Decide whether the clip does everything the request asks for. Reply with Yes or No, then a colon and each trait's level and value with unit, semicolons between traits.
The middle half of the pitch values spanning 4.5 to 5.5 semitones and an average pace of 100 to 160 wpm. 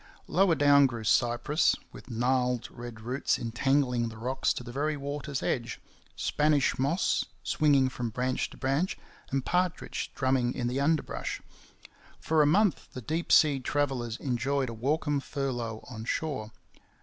No: average, 3.3 semitones; average, 150 wpm